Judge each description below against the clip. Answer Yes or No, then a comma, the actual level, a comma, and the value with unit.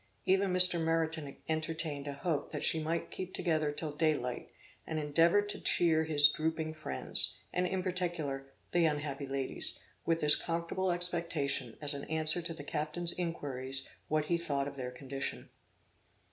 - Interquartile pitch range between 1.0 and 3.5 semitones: Yes, average, 2.9 semitones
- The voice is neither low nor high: Yes, medium, 155 Hz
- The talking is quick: No, average, 160 wpm